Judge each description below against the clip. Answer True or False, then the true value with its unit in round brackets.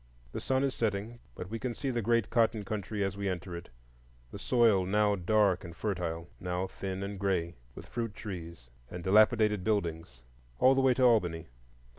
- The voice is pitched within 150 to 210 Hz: False (100 Hz)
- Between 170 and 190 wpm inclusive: True (175 wpm)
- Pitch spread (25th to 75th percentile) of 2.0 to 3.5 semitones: False (4.4 semitones)